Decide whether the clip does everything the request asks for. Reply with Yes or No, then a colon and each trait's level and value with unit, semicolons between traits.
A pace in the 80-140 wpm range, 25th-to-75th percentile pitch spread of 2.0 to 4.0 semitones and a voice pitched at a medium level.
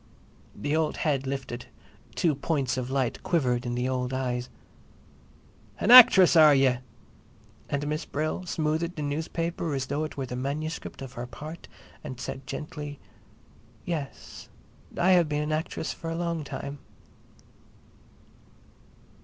Yes: slow, 135 wpm; average, 3.4 semitones; medium, 145 Hz